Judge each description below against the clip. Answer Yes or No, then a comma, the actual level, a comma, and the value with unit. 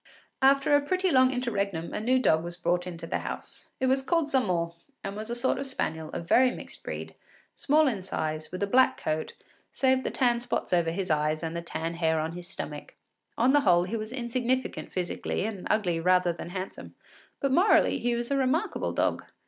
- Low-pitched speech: No, high, 205 Hz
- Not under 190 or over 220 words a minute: Yes, fast, 205 wpm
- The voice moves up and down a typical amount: No, wide, 7.3 semitones